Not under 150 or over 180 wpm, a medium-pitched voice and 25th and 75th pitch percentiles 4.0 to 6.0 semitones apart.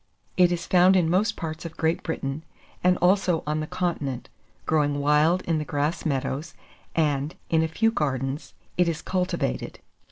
No: average, 165 wpm; medium, 160 Hz; average, 3.2 semitones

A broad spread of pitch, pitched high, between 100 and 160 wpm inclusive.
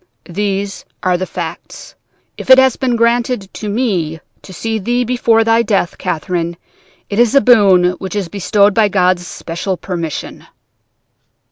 No: average, 4.3 semitones; high, 200 Hz; average, 150 wpm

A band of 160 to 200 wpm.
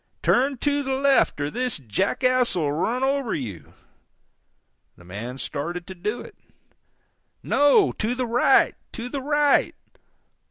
No: slow, 135 wpm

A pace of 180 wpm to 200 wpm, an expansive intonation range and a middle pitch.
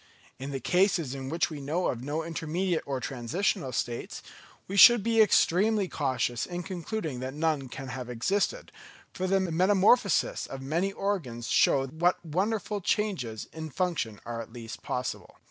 No: average, 160 wpm; wide, 6.5 semitones; medium, 160 Hz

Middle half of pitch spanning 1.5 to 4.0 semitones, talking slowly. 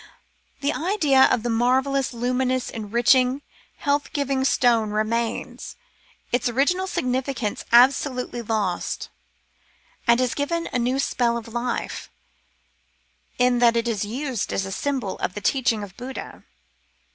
Yes: narrow, 2.5 semitones; slow, 130 wpm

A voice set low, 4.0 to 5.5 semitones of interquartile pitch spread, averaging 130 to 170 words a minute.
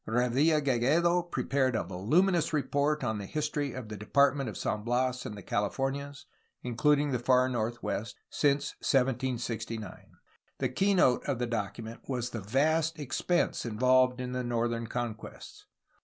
No: low, 125 Hz; average, 3.5 semitones; average, 145 wpm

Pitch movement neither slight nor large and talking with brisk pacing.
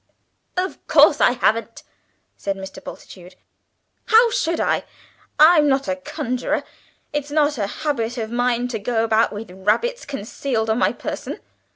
No: average, 5.0 semitones; average, 150 wpm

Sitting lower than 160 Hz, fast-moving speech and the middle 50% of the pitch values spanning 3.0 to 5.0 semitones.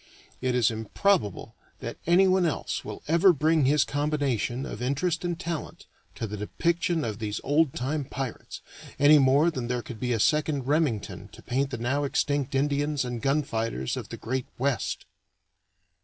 No: medium, 140 Hz; average, 170 wpm; average, 3.9 semitones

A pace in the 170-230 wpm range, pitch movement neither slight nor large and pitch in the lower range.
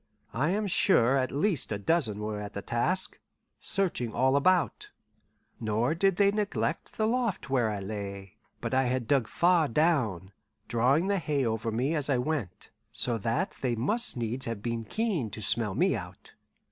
No: average, 175 wpm; wide, 7.5 semitones; low, 130 Hz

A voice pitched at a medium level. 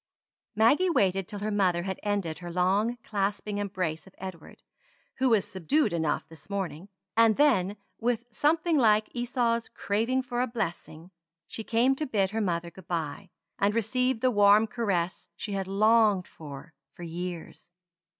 No: high, 205 Hz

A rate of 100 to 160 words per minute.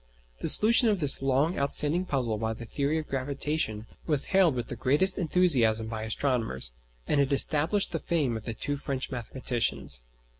No: average, 175 wpm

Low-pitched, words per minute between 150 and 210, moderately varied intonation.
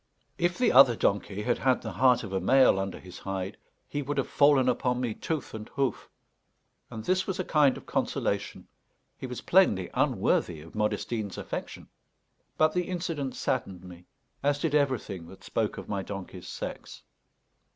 No: low, 125 Hz; average, 170 wpm; wide, 6.8 semitones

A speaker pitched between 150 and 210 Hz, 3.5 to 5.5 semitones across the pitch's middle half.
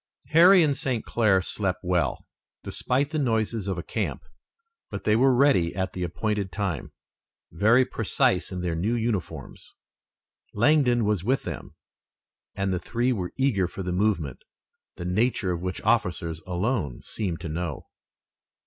No: low, 100 Hz; average, 5.2 semitones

